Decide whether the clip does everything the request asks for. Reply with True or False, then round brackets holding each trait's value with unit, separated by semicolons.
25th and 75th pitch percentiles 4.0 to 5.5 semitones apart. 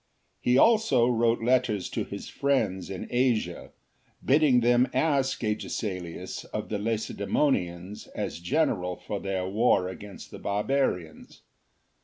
True (5.1 semitones)